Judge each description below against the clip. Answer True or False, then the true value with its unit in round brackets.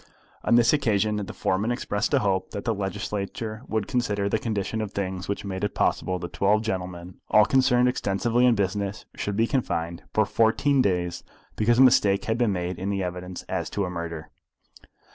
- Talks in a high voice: False (100 Hz)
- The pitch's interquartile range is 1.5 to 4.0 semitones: True (3.2 semitones)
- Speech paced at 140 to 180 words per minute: False (190 wpm)